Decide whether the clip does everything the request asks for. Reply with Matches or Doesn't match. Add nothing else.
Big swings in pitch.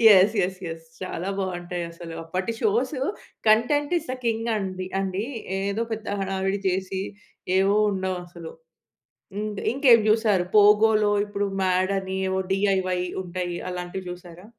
Doesn't match